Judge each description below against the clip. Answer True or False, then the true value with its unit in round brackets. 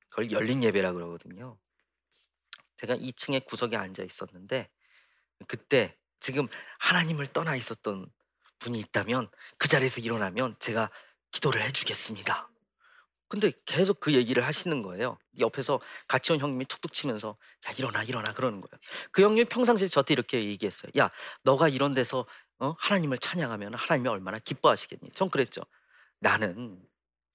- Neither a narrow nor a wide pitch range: False (5.8 semitones)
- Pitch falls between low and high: False (130 Hz)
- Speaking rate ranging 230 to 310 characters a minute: False (345 characters per minute)